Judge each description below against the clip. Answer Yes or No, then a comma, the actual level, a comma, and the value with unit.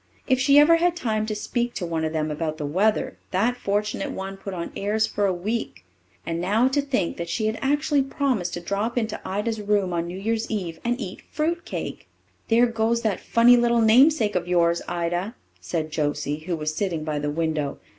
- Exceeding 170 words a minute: Yes, fast, 205 wpm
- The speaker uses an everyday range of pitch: No, wide, 5.7 semitones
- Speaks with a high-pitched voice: Yes, high, 205 Hz